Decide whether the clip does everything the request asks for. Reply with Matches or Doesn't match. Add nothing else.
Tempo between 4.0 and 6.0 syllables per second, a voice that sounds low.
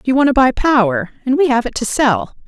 Doesn't match